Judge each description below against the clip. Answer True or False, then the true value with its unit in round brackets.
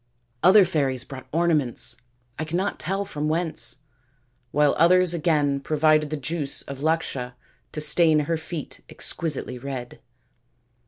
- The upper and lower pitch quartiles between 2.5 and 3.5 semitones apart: True (3.2 semitones)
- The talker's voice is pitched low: False (155 Hz)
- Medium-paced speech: False (125 wpm)